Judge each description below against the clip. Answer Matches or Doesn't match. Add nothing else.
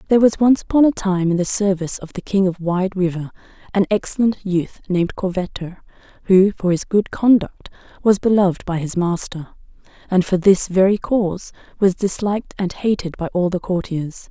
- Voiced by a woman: Matches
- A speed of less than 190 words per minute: Matches